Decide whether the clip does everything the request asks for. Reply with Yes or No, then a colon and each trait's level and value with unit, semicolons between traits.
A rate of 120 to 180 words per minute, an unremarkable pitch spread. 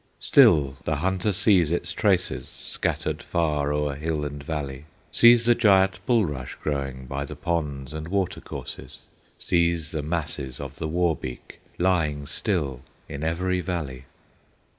Yes: average, 140 wpm; average, 4.0 semitones